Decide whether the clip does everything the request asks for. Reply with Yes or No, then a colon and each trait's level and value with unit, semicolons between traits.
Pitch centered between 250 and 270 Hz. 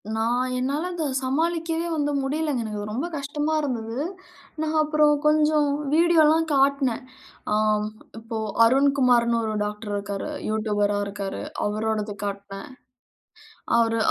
Yes: very high, 255 Hz